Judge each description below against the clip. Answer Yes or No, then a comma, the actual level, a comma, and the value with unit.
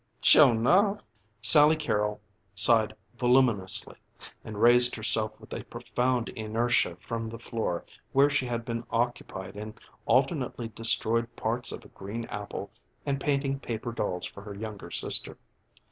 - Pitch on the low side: Yes, low, 115 Hz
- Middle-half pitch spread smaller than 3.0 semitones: Yes, narrow, 2.4 semitones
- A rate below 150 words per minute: Yes, slow, 135 wpm